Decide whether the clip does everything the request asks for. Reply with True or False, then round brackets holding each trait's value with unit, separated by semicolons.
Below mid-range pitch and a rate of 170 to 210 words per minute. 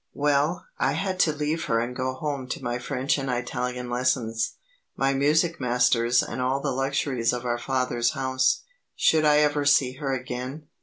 True (130 Hz; 175 wpm)